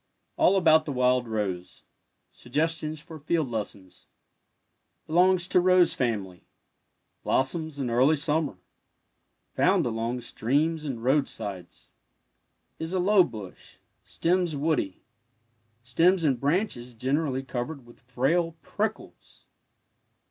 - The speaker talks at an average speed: No, slow, 105 wpm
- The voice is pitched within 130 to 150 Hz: Yes, medium, 140 Hz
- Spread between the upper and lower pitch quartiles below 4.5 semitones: No, wide, 5.4 semitones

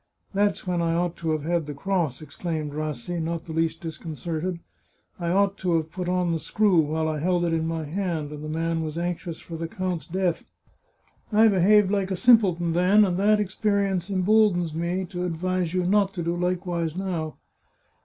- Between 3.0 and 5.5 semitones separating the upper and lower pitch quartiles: No, narrow, 2.6 semitones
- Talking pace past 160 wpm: Yes, average, 200 wpm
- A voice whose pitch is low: No, medium, 175 Hz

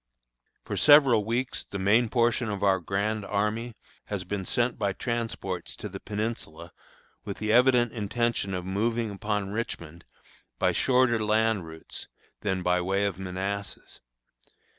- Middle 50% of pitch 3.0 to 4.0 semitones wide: Yes, average, 3.4 semitones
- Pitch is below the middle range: Yes, low, 105 Hz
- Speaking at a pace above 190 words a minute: No, average, 140 wpm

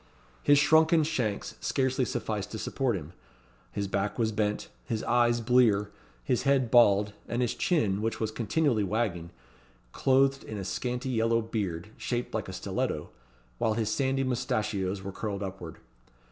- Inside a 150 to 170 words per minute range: Yes, average, 155 wpm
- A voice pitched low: Yes, low, 115 Hz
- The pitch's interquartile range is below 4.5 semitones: Yes, average, 3.9 semitones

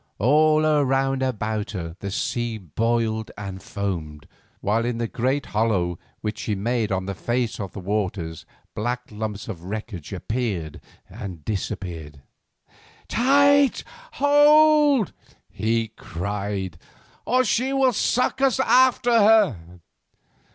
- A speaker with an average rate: No, slow, 125 wpm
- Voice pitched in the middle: No, low, 110 Hz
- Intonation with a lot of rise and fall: Yes, wide, 8.0 semitones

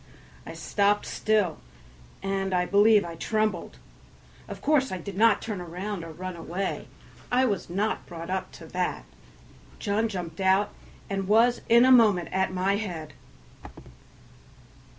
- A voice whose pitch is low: No, high, 195 Hz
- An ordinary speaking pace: Yes, average, 145 wpm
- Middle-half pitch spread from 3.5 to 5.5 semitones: No, average, 3.0 semitones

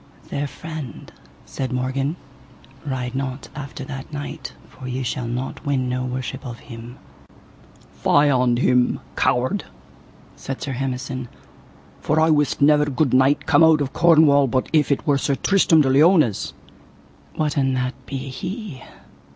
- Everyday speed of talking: Yes, average, 150 wpm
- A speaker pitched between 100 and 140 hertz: Yes, low, 135 Hz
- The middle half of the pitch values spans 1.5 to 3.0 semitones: Yes, narrow, 2.5 semitones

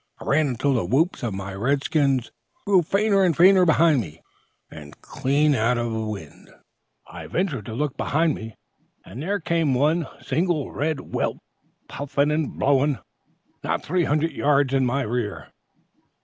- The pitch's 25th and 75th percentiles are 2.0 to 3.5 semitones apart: No, average, 4.9 semitones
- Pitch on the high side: No, medium, 140 Hz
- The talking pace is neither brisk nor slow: Yes, average, 160 wpm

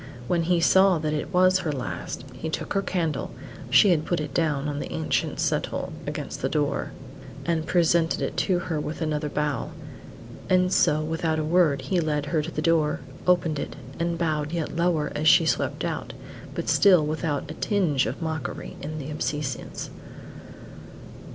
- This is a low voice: No, medium, 160 Hz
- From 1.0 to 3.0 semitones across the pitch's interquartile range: Yes, narrow, 2.5 semitones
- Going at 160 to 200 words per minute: Yes, average, 175 wpm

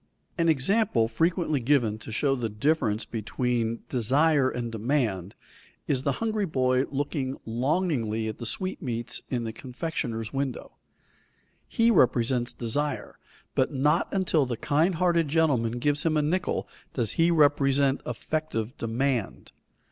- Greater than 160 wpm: No, slow, 135 wpm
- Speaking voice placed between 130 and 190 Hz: Yes, low, 135 Hz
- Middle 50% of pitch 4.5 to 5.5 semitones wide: Yes, average, 5.0 semitones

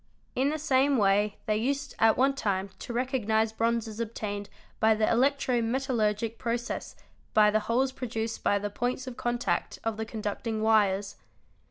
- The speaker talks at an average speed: Yes, average, 165 wpm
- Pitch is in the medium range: No, high, 225 Hz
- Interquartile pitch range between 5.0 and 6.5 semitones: No, average, 3.0 semitones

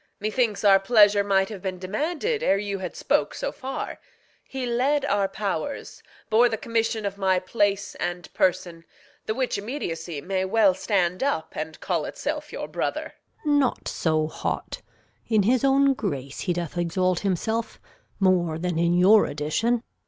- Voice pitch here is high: Yes, high, 200 Hz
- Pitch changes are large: No, average, 4.4 semitones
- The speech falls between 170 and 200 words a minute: No, average, 160 wpm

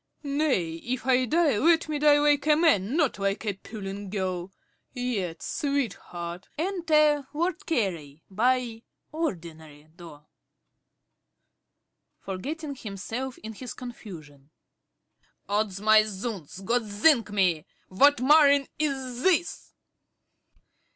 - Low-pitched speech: No, high, 230 Hz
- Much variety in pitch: Yes, wide, 7.4 semitones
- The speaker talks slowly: Yes, slow, 110 wpm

